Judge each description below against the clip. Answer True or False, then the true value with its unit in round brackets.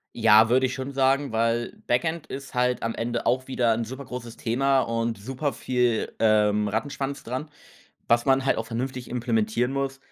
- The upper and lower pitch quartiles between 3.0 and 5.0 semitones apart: False (2.6 semitones)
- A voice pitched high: False (125 Hz)